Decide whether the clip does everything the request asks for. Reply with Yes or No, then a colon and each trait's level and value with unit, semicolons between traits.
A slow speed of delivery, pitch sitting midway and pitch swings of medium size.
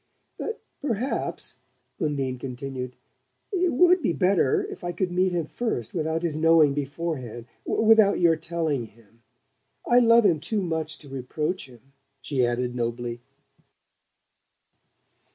No: slow, 130 wpm; medium, 155 Hz; wide, 6.4 semitones